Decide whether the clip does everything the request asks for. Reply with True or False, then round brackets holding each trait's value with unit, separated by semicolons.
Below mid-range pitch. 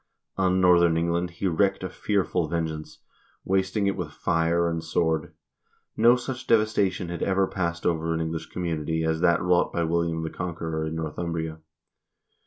True (85 Hz)